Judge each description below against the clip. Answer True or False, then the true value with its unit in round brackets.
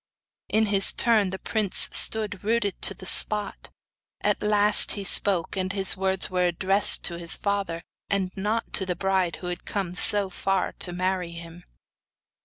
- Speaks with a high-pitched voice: True (195 Hz)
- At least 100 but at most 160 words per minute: False (170 wpm)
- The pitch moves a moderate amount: False (2.1 semitones)